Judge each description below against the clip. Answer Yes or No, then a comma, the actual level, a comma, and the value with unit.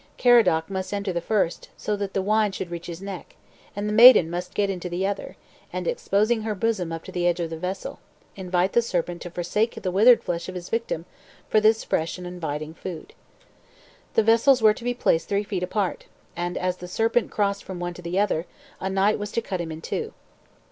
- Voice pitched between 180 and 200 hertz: Yes, high, 190 Hz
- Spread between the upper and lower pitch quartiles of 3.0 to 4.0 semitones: Yes, average, 3.3 semitones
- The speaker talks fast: Yes, fast, 215 wpm